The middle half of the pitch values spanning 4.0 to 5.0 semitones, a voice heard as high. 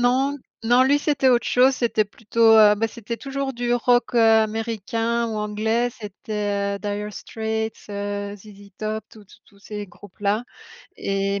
No: average, 2.7 semitones; high, 220 Hz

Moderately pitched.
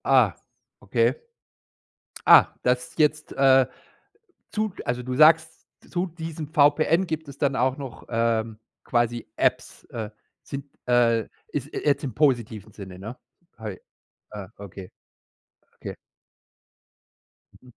No: low, 130 Hz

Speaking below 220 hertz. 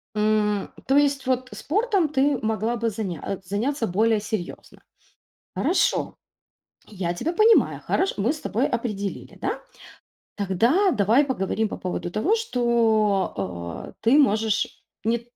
No: high, 225 Hz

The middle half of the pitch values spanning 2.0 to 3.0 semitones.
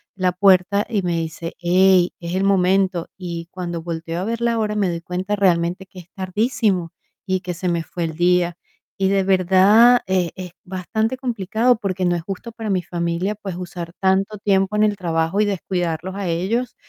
Yes: narrow, 2.6 semitones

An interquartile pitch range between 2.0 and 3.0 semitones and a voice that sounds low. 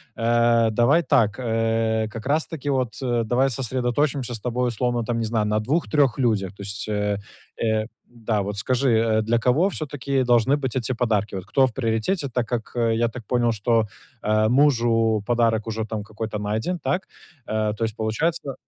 Yes: average, 2.7 semitones; low, 115 Hz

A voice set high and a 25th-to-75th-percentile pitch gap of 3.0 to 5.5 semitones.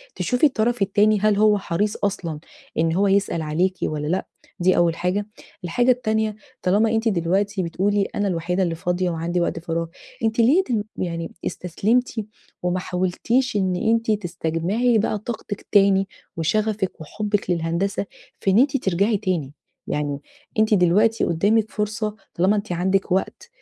Yes: high, 195 Hz; average, 3.7 semitones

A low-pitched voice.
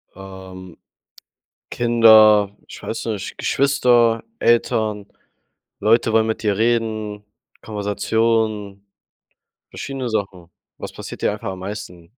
Yes: low, 110 Hz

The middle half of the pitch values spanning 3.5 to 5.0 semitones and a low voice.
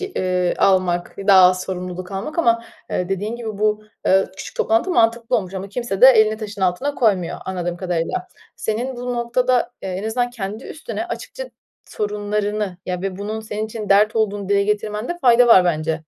No: average, 3.8 semitones; high, 210 Hz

